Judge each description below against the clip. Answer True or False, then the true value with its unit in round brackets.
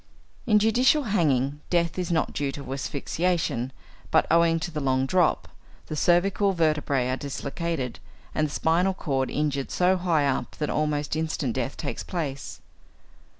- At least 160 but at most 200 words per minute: False (150 wpm)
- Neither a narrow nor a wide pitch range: True (4.1 semitones)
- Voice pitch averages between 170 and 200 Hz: False (155 Hz)